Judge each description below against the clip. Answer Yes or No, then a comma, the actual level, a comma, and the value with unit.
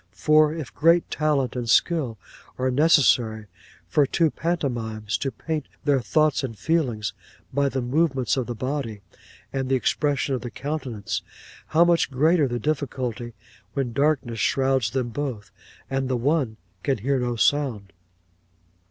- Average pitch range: Yes, average, 3.9 semitones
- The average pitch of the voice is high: No, low, 135 Hz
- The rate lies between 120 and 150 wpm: Yes, average, 145 wpm